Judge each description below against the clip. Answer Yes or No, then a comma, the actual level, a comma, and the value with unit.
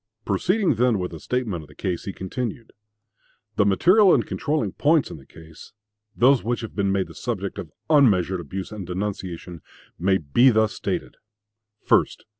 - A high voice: No, low, 100 Hz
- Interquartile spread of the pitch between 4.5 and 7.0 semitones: Yes, wide, 5.6 semitones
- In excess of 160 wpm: Yes, average, 170 wpm